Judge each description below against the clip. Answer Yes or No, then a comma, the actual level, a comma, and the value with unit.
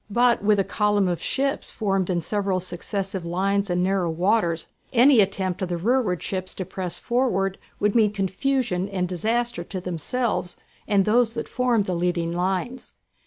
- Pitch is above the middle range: Yes, high, 195 Hz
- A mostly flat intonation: No, average, 3.8 semitones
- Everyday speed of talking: Yes, average, 165 wpm